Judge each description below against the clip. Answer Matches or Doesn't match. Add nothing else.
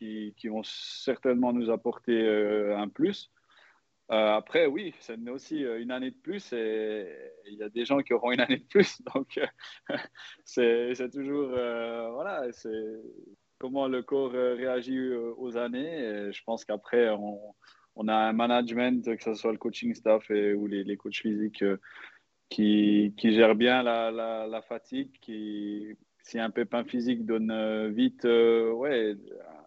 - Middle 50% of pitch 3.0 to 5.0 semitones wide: Doesn't match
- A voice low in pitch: Matches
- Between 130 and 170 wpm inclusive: Matches